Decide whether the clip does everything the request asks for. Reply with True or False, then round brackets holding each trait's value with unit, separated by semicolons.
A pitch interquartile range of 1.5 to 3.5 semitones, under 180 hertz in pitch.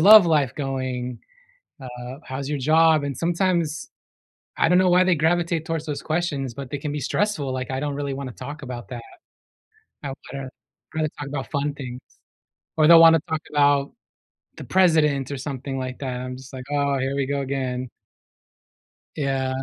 True (3.2 semitones; 140 Hz)